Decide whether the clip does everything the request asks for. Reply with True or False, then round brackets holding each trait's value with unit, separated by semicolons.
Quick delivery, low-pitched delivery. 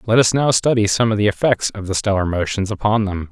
True (255 wpm; 105 Hz)